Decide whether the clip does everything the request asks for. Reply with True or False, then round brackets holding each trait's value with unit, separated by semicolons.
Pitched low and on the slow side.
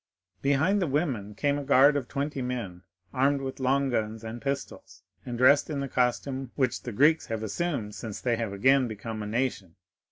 False (130 Hz; 190 wpm)